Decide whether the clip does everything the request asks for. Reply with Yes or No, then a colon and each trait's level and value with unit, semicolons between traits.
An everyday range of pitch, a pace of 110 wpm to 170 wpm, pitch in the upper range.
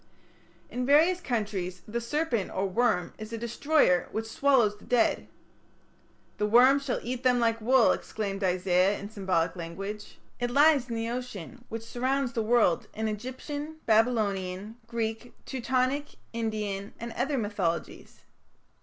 Yes: average, 3.8 semitones; average, 140 wpm; high, 230 Hz